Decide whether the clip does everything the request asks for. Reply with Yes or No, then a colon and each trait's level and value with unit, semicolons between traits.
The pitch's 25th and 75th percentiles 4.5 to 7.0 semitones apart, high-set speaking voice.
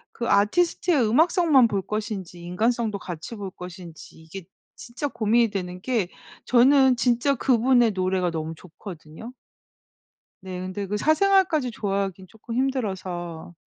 Yes: wide, 5.4 semitones; high, 210 Hz